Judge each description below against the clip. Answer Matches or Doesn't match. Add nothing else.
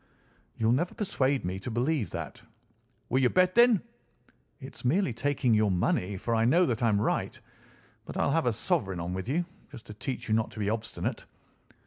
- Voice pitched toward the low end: Matches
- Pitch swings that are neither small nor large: Matches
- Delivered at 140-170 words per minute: Doesn't match